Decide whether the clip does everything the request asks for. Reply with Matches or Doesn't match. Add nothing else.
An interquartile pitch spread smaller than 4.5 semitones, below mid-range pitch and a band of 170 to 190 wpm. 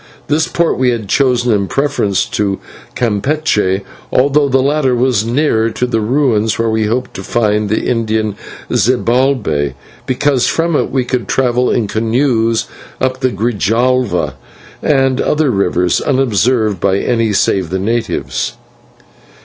Doesn't match